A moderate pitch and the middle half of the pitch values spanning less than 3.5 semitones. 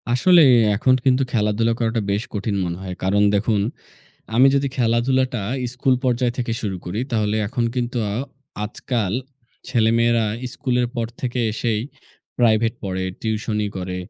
No: low, 115 Hz; average, 2.9 semitones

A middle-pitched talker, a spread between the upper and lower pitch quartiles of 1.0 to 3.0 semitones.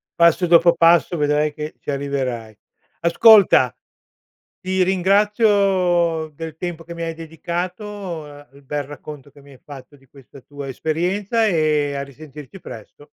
No: medium, 160 Hz; average, 3.8 semitones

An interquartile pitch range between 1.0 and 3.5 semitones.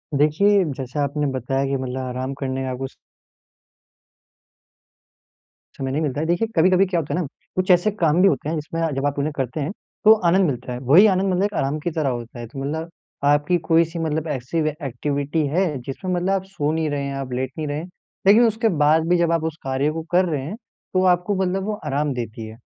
No: average, 4.6 semitones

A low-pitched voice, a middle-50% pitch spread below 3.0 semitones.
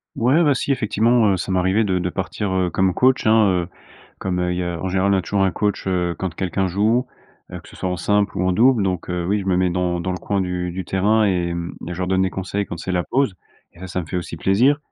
Yes: very low, 95 Hz; narrow, 2.5 semitones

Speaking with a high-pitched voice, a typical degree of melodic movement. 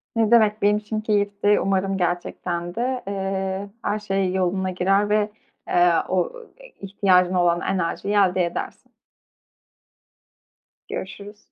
No: high, 195 Hz; narrow, 2.2 semitones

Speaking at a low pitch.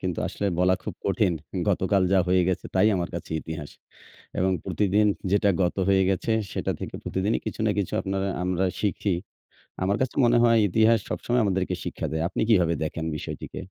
Yes: very low, 95 Hz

